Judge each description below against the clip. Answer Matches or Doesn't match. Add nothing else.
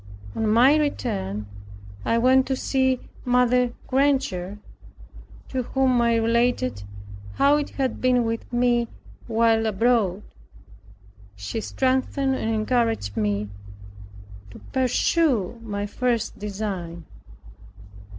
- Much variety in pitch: Doesn't match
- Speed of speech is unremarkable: Doesn't match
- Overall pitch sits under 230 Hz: Doesn't match